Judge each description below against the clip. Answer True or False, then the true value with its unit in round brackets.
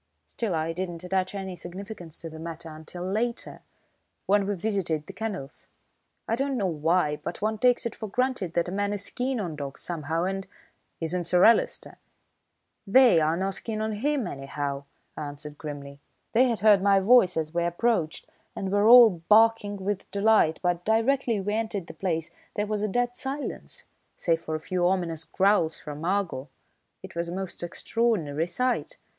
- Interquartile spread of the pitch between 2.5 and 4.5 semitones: False (4.9 semitones)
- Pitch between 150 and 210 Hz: True (190 Hz)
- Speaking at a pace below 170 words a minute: False (180 wpm)